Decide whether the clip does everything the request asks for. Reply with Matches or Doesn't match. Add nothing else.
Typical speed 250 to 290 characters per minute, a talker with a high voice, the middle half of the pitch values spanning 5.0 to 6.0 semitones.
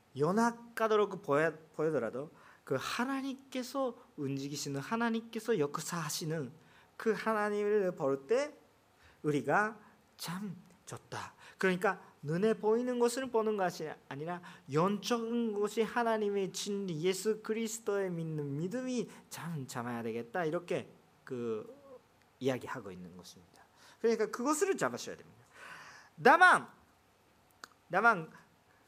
Doesn't match